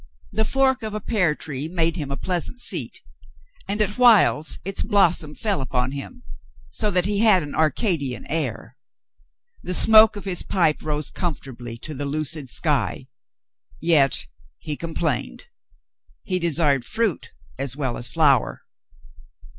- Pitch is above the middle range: No, medium, 160 Hz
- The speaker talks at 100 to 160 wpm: Yes, average, 145 wpm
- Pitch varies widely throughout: Yes, wide, 6.1 semitones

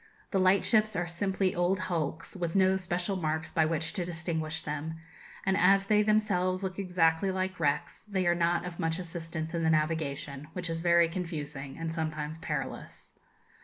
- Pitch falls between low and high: Yes, medium, 170 Hz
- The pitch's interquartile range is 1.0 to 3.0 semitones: Yes, narrow, 2.6 semitones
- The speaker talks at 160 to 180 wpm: Yes, average, 170 wpm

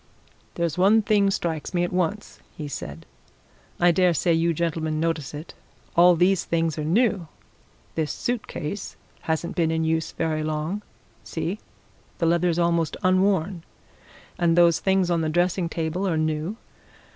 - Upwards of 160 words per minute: No, average, 155 wpm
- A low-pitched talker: No, medium, 170 Hz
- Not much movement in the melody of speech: Yes, narrow, 2.3 semitones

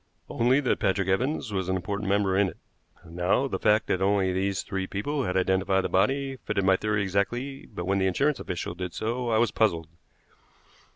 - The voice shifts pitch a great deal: No, average, 3.7 semitones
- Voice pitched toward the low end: Yes, low, 100 Hz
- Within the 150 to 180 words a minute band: No, average, 195 wpm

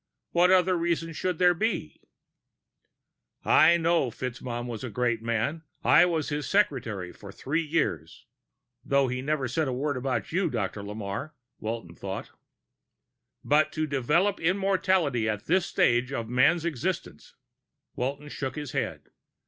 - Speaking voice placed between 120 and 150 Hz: Yes, medium, 140 Hz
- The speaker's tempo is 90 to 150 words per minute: Yes, average, 140 wpm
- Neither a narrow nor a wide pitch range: No, wide, 6.0 semitones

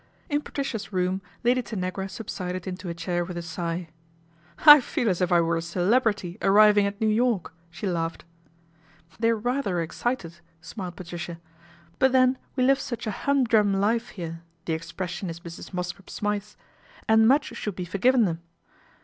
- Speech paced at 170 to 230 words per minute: Yes, average, 175 wpm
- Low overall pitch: No, high, 190 Hz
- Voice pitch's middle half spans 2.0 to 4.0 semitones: No, average, 4.7 semitones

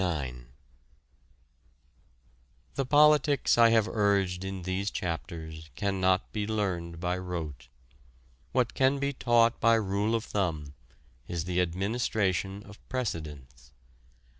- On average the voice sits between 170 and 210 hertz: No, very low, 95 Hz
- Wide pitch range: No, average, 4.9 semitones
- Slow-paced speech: Yes, slow, 110 wpm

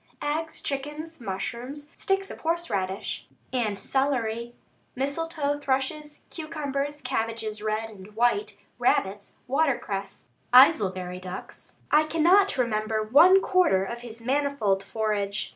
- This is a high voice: Yes, very high, 255 Hz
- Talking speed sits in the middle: No, slow, 110 wpm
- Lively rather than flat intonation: Yes, wide, 5.7 semitones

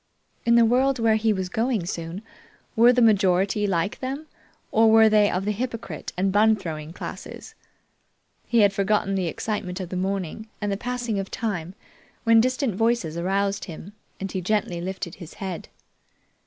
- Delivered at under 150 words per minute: No, average, 170 wpm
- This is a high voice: Yes, high, 200 Hz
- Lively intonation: No, average, 3.4 semitones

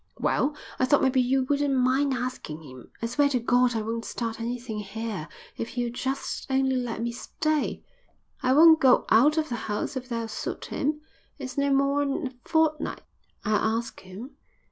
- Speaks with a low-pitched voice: No, very high, 255 Hz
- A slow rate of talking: No, average, 180 wpm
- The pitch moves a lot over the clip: No, average, 3.4 semitones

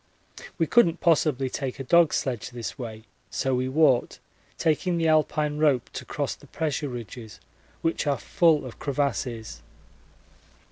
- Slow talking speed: No, average, 145 wpm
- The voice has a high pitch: No, medium, 140 Hz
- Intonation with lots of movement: No, average, 4.1 semitones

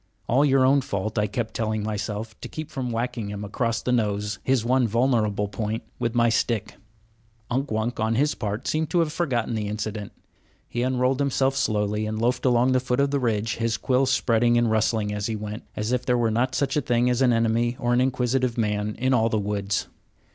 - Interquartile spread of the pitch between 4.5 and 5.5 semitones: No, average, 2.9 semitones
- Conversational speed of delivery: No, fast, 215 wpm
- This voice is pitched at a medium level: No, low, 115 Hz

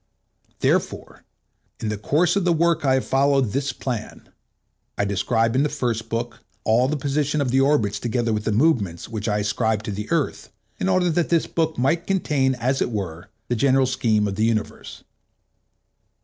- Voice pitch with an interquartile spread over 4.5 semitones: Yes, average, 5.2 semitones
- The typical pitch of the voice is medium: No, low, 125 Hz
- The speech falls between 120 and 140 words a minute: No, average, 185 wpm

